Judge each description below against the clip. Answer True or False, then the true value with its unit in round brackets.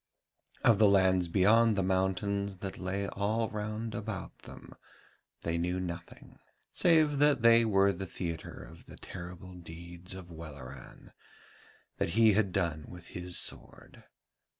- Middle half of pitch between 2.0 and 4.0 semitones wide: True (3.5 semitones)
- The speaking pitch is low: True (95 Hz)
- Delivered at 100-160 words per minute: True (140 wpm)